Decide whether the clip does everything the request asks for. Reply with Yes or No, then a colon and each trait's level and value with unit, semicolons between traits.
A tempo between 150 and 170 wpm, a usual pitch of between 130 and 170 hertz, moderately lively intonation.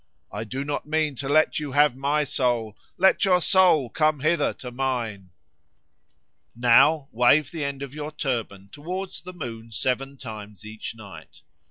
Yes: average, 160 wpm; low, 135 Hz; average, 4.7 semitones